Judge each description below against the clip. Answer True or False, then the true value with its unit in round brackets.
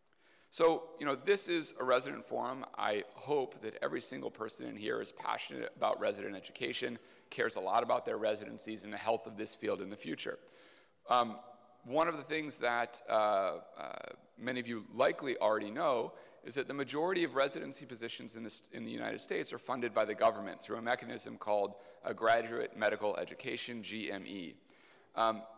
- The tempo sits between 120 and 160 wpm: False (185 wpm)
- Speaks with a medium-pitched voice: False (120 Hz)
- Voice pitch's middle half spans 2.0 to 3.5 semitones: False (5.4 semitones)